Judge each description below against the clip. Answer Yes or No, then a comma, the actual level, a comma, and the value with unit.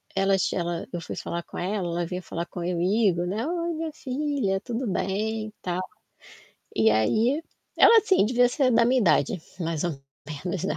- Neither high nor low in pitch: No, high, 195 Hz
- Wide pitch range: Yes, wide, 6.0 semitones